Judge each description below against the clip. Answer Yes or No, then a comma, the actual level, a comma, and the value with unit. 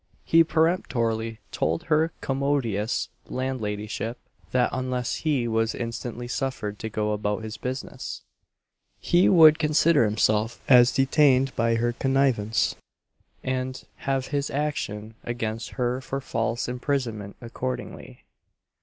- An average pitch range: Yes, average, 3.4 semitones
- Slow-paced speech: Yes, slow, 115 wpm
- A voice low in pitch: Yes, low, 125 Hz